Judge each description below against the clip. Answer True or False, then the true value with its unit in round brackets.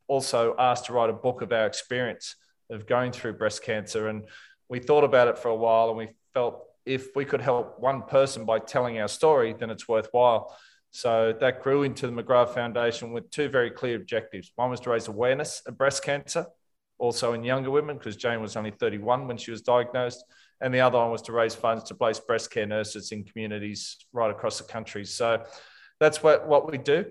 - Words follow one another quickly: True (215 wpm)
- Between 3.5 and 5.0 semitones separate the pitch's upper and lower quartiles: False (2.7 semitones)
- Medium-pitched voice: False (120 Hz)